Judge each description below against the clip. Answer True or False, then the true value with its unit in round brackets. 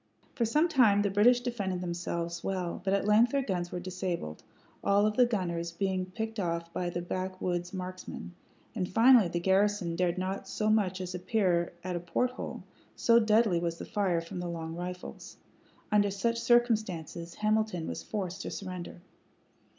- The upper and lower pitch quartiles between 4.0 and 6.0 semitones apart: False (3.5 semitones)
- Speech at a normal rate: True (175 wpm)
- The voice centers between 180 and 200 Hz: True (185 Hz)